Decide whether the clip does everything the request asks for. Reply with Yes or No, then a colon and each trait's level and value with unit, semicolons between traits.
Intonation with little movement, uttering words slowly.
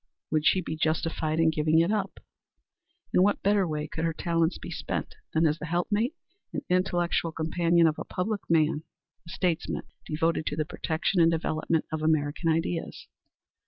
No: narrow, 1.8 semitones; average, 170 wpm